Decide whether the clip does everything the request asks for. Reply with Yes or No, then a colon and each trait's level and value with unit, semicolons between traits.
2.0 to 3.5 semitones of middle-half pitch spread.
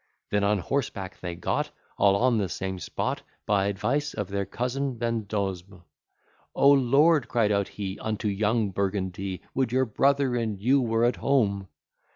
No: average, 4.2 semitones